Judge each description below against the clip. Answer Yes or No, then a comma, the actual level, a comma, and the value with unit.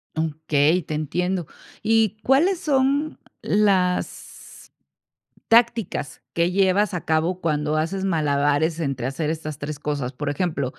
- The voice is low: No, medium, 165 Hz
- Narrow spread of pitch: No, average, 4.8 semitones